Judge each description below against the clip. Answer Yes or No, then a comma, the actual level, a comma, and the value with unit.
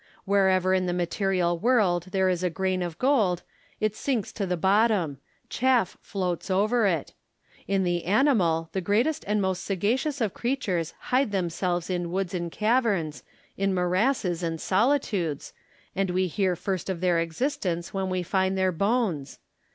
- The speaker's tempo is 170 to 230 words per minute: No, average, 160 wpm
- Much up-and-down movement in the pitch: No, average, 3.2 semitones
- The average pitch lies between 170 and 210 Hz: Yes, high, 190 Hz